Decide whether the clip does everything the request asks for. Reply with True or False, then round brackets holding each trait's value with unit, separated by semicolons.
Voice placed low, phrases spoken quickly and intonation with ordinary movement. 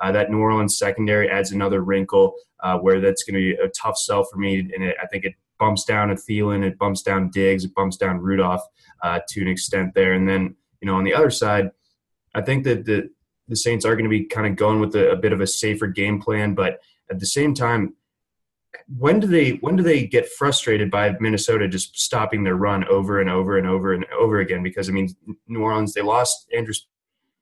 False (100 Hz; 235 wpm; 2.3 semitones)